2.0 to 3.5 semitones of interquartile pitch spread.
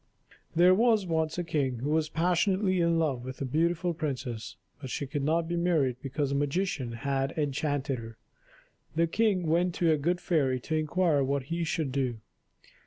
No: average, 4.0 semitones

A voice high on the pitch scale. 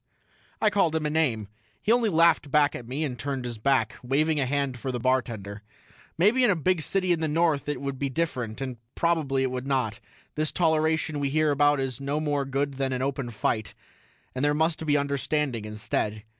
No: medium, 140 Hz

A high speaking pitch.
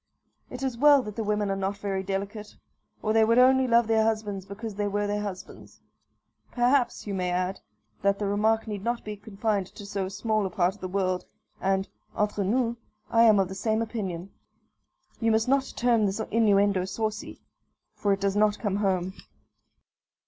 Yes: high, 210 Hz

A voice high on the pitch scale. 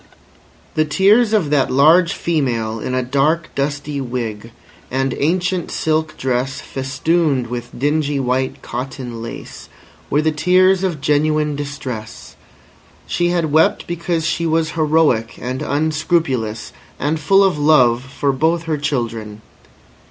No: medium, 145 Hz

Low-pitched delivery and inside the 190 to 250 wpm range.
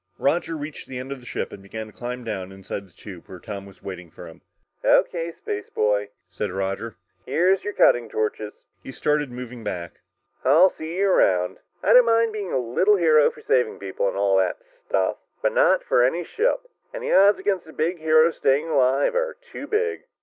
Yes: low, 130 Hz; average, 200 wpm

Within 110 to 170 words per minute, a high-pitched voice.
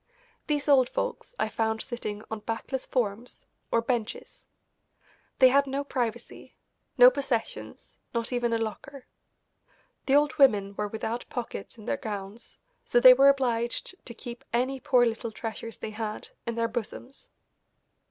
Yes: average, 150 wpm; high, 240 Hz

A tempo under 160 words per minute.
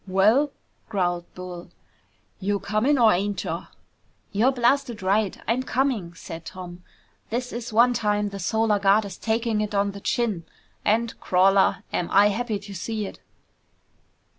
Yes: average, 150 wpm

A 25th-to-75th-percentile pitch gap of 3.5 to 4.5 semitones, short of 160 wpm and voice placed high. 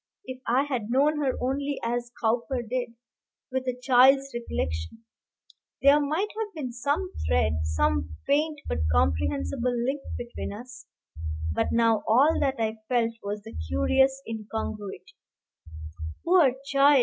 Yes: average, 4.2 semitones; slow, 135 wpm; high, 245 Hz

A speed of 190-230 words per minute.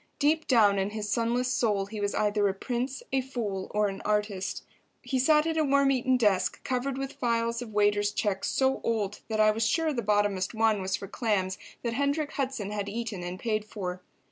Yes: fast, 205 wpm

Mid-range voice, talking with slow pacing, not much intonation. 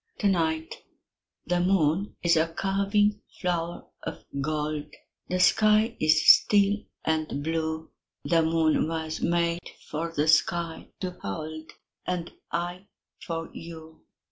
Yes: medium, 165 Hz; slow, 120 wpm; narrow, 2.3 semitones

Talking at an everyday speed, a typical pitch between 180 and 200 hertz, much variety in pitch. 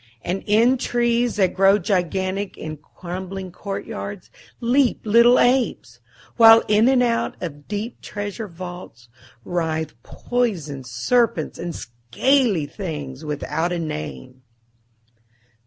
No: slow, 110 wpm; high, 190 Hz; wide, 6.5 semitones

